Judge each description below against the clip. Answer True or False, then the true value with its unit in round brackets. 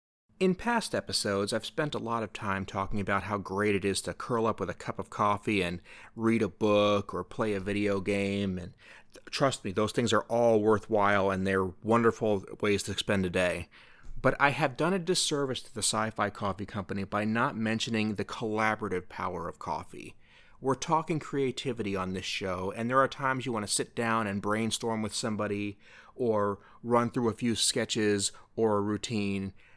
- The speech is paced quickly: False (190 wpm)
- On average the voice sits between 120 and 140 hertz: False (105 Hz)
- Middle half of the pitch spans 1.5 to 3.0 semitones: True (2.7 semitones)